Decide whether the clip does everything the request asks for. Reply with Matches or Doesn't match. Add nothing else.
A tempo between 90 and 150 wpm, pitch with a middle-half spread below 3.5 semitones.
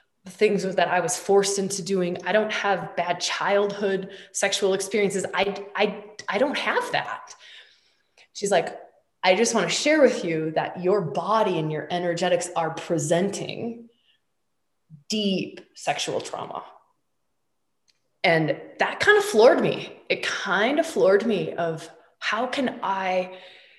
Matches